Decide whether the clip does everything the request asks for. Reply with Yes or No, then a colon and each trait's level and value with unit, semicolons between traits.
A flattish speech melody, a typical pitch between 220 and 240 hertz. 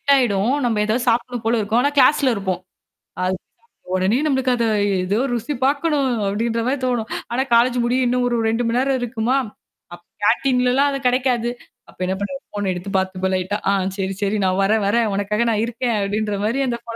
No: average, 3.7 semitones; high, 235 Hz